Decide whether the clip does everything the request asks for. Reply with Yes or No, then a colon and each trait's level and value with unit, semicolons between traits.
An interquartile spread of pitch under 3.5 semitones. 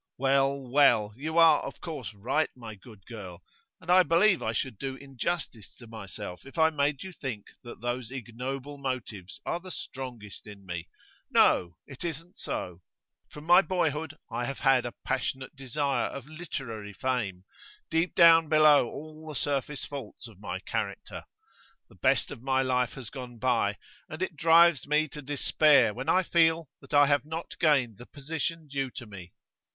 No: average, 4.9 semitones